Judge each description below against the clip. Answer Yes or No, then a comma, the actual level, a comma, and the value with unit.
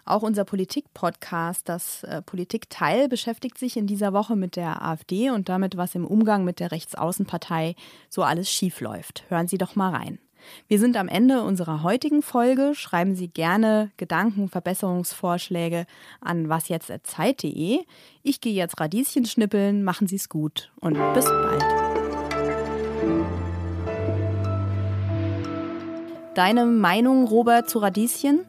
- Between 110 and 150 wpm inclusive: Yes, slow, 125 wpm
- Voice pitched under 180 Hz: No, high, 190 Hz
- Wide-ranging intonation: Yes, wide, 6.0 semitones